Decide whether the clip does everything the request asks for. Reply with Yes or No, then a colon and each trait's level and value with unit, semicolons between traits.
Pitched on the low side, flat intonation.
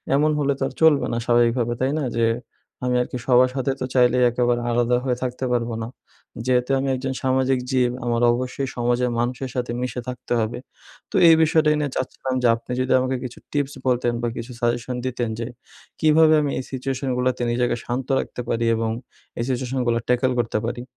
Yes: low, 125 Hz; narrow, 1.6 semitones